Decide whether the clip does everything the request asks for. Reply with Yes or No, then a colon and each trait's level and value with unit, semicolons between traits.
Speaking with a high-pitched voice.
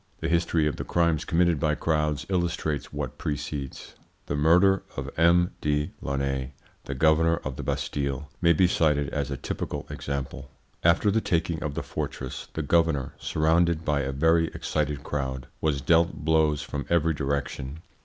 No: very low, 75 Hz